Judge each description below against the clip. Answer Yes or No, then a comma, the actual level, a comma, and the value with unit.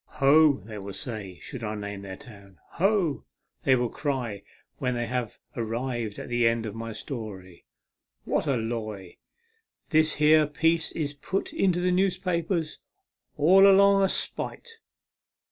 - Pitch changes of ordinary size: No, wide, 7.0 semitones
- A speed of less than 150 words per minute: No, average, 165 wpm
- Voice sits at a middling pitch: No, low, 130 Hz